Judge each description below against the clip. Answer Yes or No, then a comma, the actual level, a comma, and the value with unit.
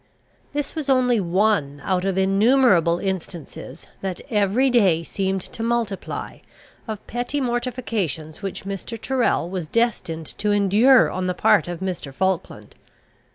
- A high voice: Yes, high, 195 Hz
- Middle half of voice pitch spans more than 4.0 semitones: Yes, average, 4.8 semitones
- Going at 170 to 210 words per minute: No, slow, 135 wpm